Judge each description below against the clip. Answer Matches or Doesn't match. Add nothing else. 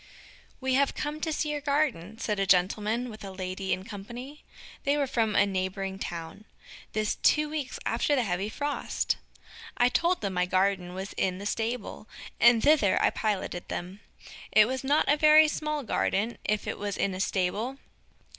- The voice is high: Matches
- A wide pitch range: Matches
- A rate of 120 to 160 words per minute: Doesn't match